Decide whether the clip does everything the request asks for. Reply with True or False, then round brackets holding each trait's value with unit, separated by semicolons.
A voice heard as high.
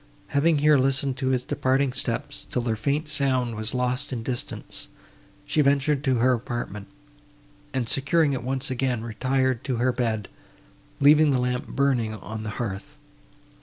False (130 Hz)